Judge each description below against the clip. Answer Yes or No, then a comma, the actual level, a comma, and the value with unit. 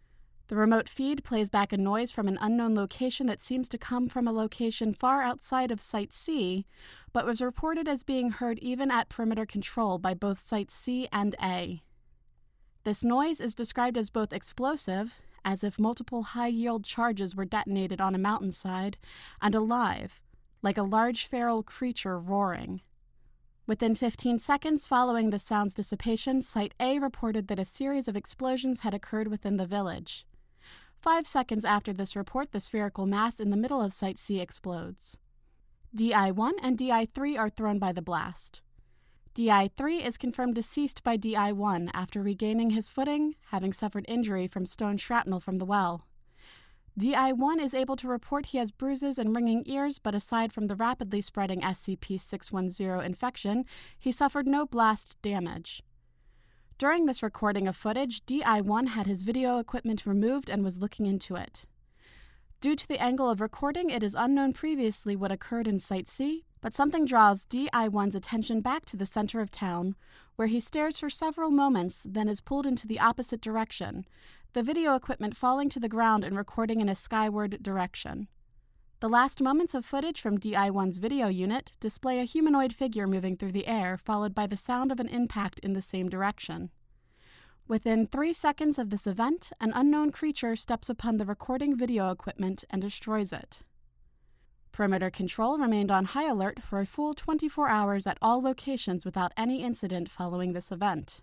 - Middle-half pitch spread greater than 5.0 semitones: No, average, 4.2 semitones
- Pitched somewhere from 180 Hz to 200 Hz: No, high, 220 Hz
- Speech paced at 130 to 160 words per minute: No, average, 175 wpm